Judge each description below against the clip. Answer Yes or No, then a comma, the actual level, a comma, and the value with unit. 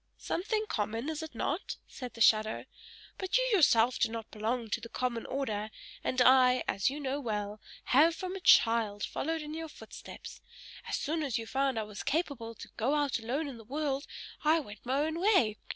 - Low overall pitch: No, very high, 260 Hz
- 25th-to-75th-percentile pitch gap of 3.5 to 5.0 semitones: No, wide, 5.4 semitones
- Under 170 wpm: No, average, 200 wpm